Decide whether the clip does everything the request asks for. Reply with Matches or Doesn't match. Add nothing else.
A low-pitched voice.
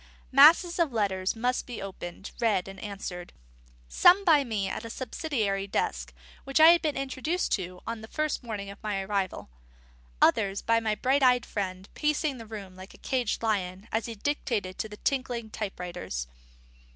Doesn't match